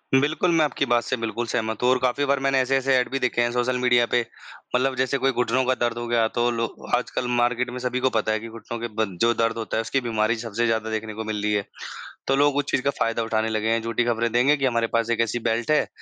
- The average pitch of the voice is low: Yes, low, 120 Hz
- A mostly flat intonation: Yes, narrow, 2.1 semitones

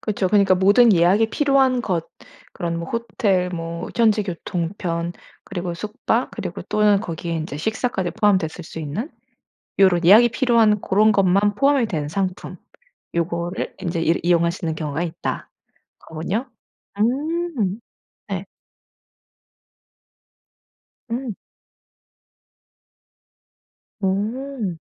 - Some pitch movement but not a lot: Yes, average, 4.5 semitones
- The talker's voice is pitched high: Yes, high, 195 Hz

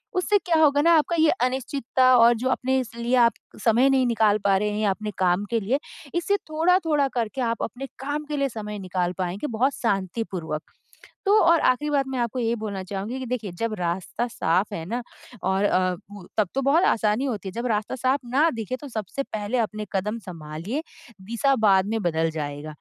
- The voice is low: No, high, 230 Hz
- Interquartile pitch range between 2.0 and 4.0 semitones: No, wide, 5.4 semitones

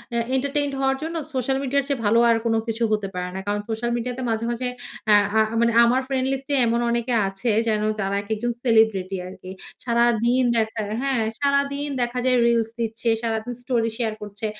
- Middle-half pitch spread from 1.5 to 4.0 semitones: Yes, average, 2.8 semitones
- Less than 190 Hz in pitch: No, high, 235 Hz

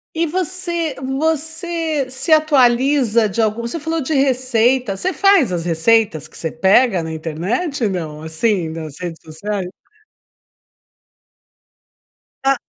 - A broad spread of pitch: Yes, wide, 9.0 semitones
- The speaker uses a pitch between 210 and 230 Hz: No, high, 245 Hz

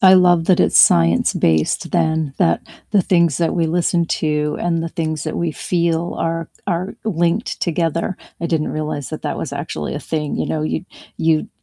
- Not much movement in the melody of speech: Yes, narrow, 2.0 semitones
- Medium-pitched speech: Yes, medium, 165 Hz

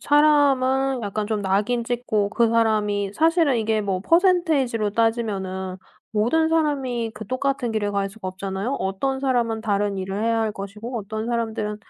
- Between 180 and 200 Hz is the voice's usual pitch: No, high, 225 Hz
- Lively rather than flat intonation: No, average, 4.1 semitones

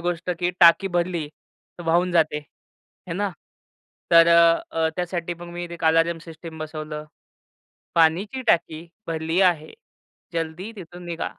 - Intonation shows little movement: Yes, narrow, 1.5 semitones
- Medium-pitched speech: Yes, medium, 170 Hz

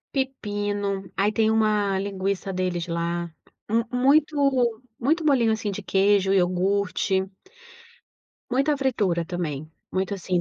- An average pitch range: Yes, average, 3.9 semitones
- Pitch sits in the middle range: No, high, 200 Hz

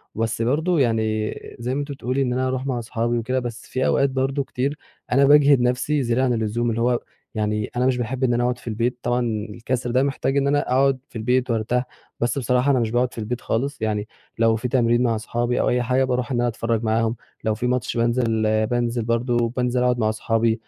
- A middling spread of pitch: No, narrow, 2.1 semitones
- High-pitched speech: No, low, 120 Hz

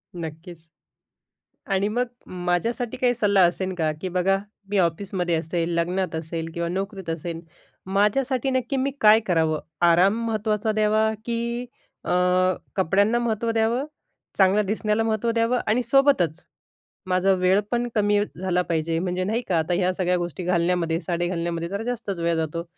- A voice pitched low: No, high, 190 Hz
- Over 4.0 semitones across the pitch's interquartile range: Yes, average, 4.4 semitones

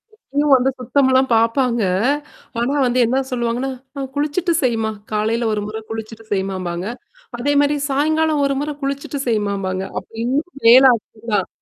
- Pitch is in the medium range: No, high, 245 Hz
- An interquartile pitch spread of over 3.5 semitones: Yes, average, 4.1 semitones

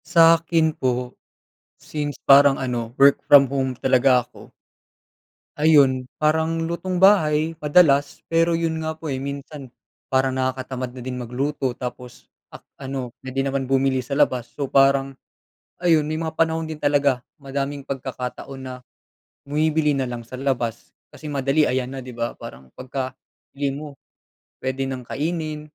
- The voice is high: No, medium, 140 Hz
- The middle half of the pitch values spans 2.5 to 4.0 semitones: Yes, average, 2.9 semitones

